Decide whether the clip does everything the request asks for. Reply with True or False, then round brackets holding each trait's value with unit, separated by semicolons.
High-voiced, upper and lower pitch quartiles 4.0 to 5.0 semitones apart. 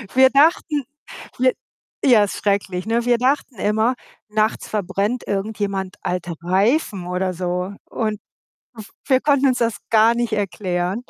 True (215 Hz; 4.4 semitones)